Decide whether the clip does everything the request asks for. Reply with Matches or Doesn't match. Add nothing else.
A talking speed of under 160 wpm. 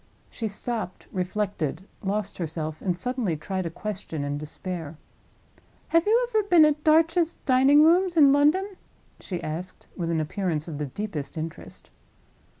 Matches